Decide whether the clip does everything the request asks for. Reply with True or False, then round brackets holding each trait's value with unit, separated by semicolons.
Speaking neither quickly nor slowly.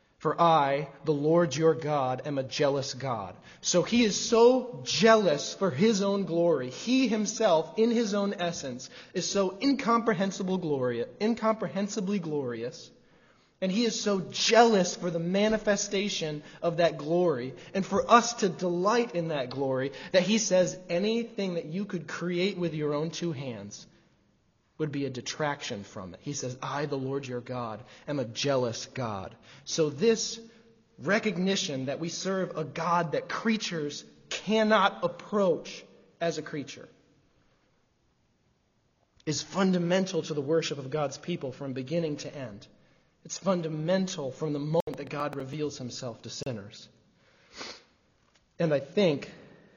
True (145 wpm)